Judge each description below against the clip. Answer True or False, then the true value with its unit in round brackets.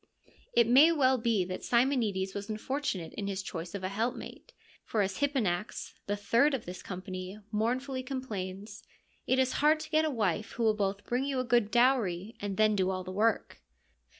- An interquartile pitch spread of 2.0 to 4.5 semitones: False (5.0 semitones)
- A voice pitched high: True (215 Hz)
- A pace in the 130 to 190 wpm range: False (200 wpm)